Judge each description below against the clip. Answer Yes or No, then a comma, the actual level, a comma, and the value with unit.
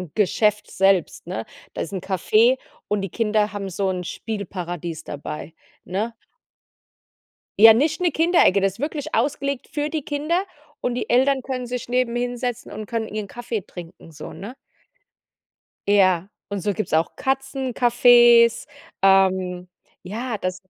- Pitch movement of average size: Yes, average, 4.7 semitones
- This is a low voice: No, high, 215 Hz